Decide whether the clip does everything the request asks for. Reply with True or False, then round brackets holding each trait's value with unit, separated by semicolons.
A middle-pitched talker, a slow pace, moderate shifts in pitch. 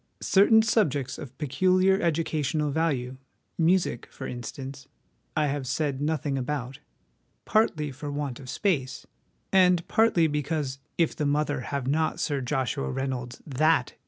True (145 Hz; 130 wpm; 3.5 semitones)